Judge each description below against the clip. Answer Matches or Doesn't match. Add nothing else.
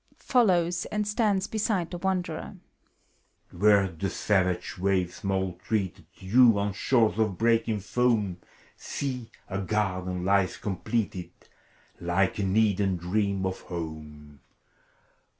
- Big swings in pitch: Doesn't match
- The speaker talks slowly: Matches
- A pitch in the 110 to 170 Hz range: Doesn't match